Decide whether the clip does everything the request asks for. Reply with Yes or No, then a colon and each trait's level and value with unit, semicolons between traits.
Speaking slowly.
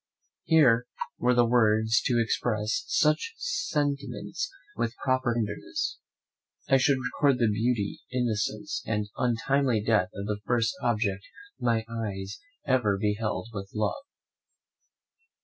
Yes: slow, 115 wpm